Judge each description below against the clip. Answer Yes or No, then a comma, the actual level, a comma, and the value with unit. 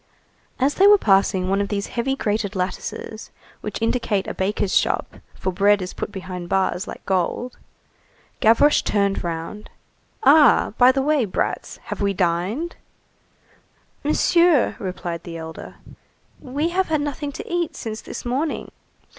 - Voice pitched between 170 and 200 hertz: No, high, 210 Hz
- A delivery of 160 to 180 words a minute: No, average, 145 wpm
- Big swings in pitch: Yes, wide, 6.9 semitones